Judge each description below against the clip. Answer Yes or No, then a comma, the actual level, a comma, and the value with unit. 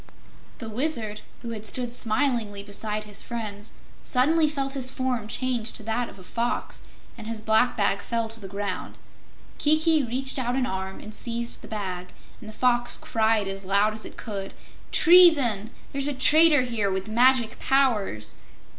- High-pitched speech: Yes, high, 230 Hz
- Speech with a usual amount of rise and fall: Yes, average, 3.7 semitones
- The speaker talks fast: No, average, 170 wpm